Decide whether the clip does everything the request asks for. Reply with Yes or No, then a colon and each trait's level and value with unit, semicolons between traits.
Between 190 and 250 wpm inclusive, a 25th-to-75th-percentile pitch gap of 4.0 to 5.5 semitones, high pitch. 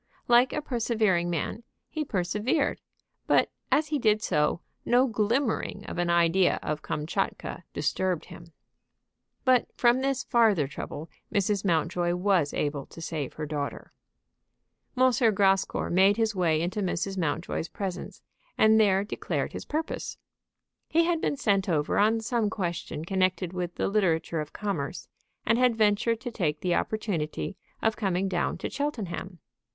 No: average, 145 wpm; average, 4.7 semitones; high, 195 Hz